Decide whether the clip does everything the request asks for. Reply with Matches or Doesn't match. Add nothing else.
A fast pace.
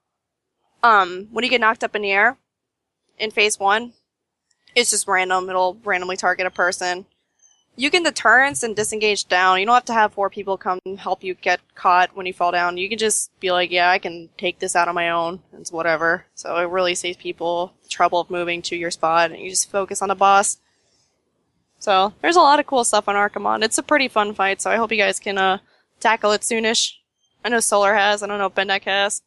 Matches